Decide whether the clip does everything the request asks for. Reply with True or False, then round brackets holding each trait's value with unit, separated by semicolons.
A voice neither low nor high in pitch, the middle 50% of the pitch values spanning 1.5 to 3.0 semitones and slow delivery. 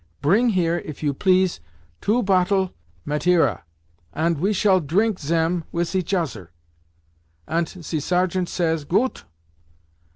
True (175 Hz; 2.7 semitones; 125 wpm)